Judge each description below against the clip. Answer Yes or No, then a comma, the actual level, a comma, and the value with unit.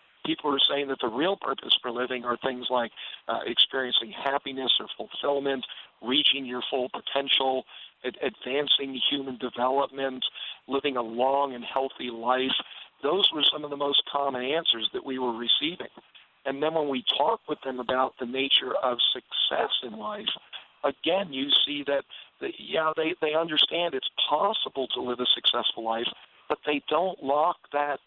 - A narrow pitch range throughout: Yes, narrow, 2.3 semitones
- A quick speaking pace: No, average, 165 wpm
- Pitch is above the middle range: No, low, 135 Hz